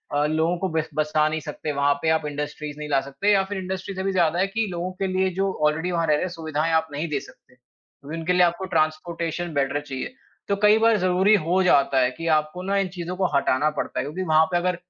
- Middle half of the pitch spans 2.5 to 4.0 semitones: Yes, average, 3.5 semitones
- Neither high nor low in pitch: Yes, medium, 165 Hz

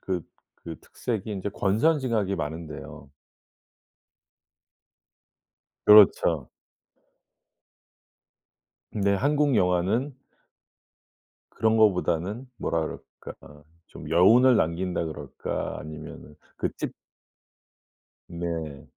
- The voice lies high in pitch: No, very low, 95 Hz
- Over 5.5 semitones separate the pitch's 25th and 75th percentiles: No, average, 5.2 semitones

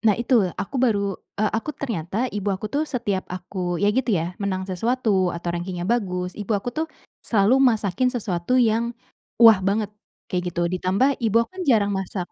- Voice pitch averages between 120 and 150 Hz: No, high, 205 Hz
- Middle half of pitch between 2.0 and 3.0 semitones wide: No, average, 4.2 semitones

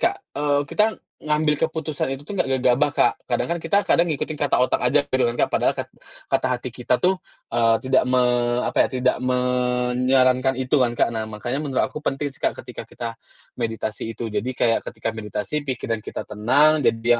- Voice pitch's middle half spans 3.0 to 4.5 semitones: Yes, average, 3.3 semitones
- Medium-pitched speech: No, low, 130 Hz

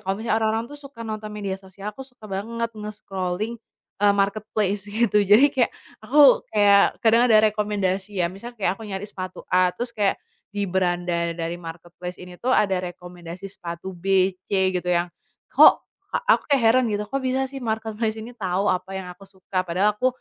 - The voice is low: No, high, 205 Hz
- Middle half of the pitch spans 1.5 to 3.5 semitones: Yes, average, 3.1 semitones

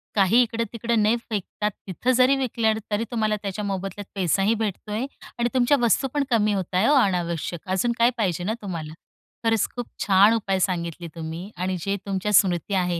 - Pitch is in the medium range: No, high, 205 Hz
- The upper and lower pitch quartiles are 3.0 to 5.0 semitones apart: Yes, average, 3.7 semitones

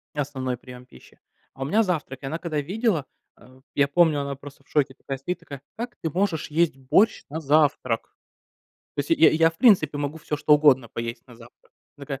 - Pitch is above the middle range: No, medium, 145 Hz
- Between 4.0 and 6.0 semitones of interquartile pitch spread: No, average, 3.4 semitones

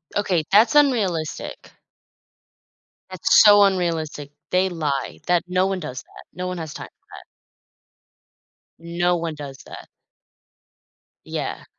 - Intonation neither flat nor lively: Yes, average, 3.2 semitones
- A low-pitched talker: No, medium, 175 Hz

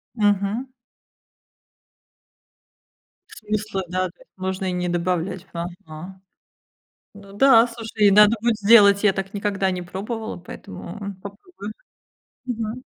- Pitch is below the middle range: No, high, 200 Hz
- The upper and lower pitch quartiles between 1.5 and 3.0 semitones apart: Yes, narrow, 2.6 semitones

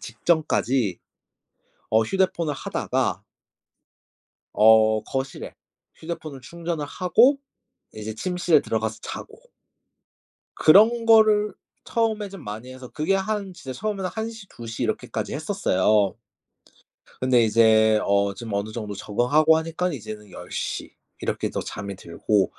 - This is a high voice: No, low, 130 Hz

